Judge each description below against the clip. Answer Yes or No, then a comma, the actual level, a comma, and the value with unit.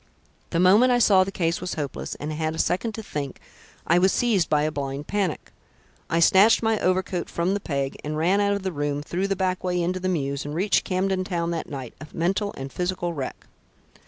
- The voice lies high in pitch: No, medium, 180 Hz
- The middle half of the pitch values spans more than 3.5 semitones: Yes, average, 3.9 semitones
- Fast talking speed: Yes, fast, 220 wpm